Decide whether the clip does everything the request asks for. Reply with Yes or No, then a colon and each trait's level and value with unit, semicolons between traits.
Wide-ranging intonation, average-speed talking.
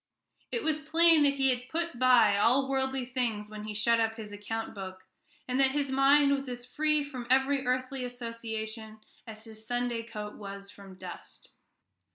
No: average, 3.7 semitones; average, 180 wpm